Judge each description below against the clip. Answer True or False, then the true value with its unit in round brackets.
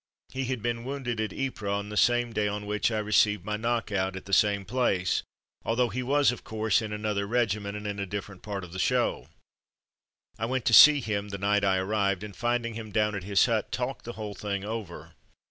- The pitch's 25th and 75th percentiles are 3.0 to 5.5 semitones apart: False (2.6 semitones)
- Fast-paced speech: True (230 wpm)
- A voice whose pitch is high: False (105 Hz)